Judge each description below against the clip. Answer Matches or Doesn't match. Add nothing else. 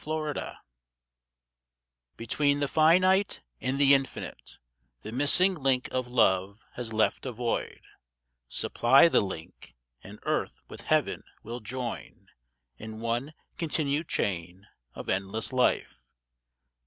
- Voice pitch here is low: Matches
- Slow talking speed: Matches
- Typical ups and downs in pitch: Matches